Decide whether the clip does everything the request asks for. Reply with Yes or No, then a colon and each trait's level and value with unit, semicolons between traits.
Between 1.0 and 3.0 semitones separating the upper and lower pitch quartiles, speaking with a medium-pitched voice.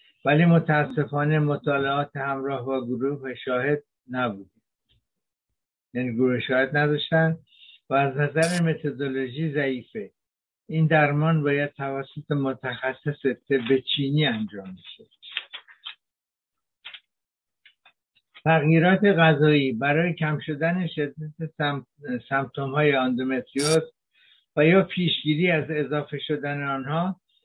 Yes: average, 2.7 semitones; medium, 145 Hz